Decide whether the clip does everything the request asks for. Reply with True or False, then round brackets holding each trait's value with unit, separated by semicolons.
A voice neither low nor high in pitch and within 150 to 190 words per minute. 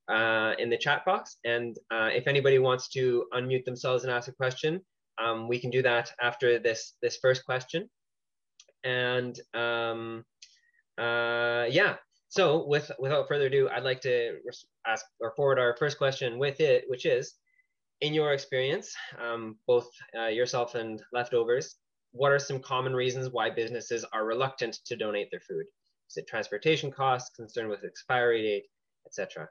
False (130 Hz; 165 wpm)